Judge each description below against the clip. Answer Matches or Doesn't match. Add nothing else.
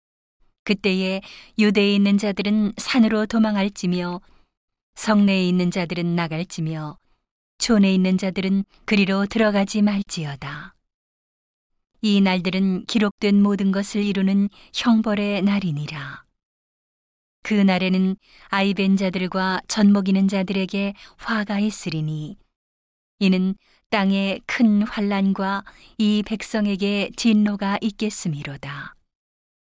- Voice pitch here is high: Matches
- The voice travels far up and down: Doesn't match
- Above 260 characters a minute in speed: Doesn't match